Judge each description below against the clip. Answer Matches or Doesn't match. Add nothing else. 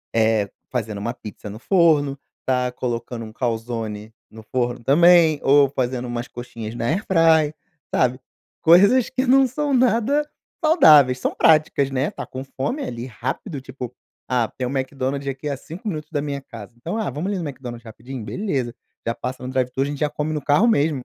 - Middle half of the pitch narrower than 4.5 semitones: Doesn't match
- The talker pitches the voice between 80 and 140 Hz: Matches